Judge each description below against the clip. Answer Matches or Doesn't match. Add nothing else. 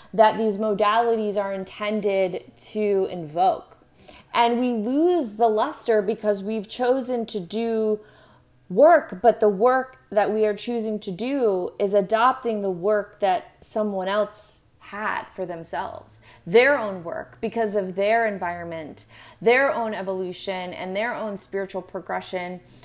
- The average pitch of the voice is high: Matches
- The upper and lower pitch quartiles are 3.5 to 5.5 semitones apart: Doesn't match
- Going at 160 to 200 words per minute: Doesn't match